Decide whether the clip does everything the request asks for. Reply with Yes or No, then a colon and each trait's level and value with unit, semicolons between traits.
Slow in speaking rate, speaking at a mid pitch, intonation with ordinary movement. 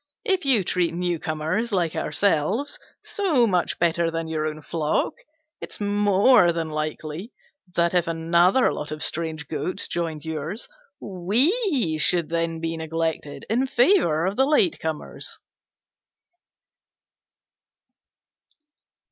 Yes: slow, 115 wpm; medium, 170 Hz; average, 4.4 semitones